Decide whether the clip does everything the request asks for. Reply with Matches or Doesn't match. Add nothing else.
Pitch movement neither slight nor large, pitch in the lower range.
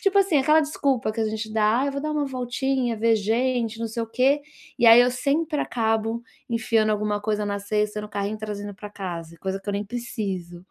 Doesn't match